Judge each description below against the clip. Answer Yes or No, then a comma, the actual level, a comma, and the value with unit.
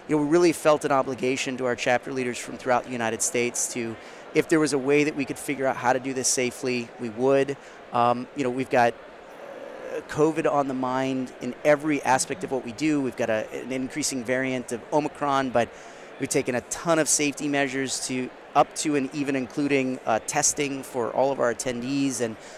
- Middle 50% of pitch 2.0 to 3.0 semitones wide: Yes, narrow, 2.6 semitones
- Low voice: Yes, low, 130 Hz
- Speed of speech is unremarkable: No, fast, 215 wpm